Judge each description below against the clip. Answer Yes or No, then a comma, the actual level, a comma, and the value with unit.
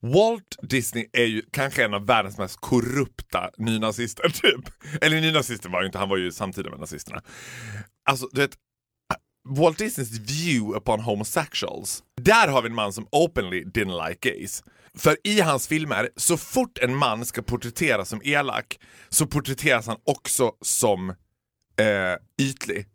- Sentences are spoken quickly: No, average, 155 wpm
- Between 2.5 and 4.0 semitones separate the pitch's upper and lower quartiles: No, average, 5.0 semitones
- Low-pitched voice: Yes, low, 125 Hz